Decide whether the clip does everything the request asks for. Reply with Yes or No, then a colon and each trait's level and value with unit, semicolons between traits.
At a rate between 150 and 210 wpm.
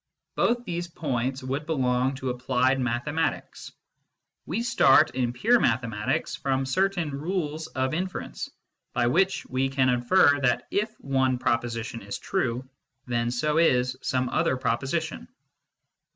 No: slow, 135 wpm